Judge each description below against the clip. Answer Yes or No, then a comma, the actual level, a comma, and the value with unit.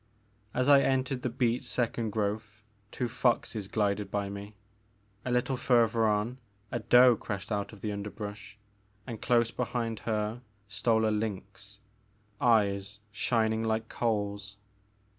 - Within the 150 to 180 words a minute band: No, slow, 135 wpm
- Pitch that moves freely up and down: No, average, 2.7 semitones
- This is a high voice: No, low, 110 Hz